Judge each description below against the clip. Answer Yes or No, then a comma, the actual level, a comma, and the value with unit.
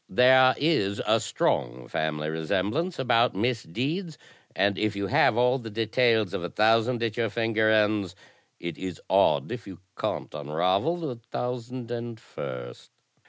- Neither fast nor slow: Yes, average, 150 wpm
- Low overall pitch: Yes, low, 110 Hz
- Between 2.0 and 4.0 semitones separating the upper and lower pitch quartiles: No, average, 4.7 semitones